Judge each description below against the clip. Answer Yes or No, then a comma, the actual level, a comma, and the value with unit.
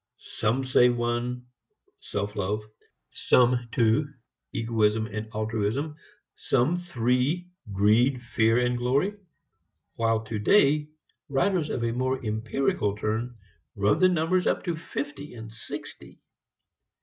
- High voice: No, low, 120 Hz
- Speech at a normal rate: No, slow, 115 wpm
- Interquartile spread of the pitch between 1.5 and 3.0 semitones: No, average, 4.0 semitones